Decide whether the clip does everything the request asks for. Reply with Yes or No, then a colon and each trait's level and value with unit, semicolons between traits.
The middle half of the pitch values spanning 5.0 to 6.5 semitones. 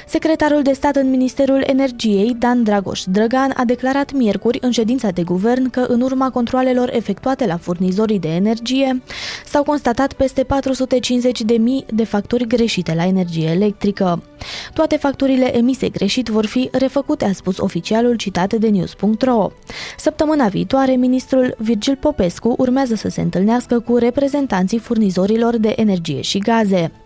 No: average, 4.3 semitones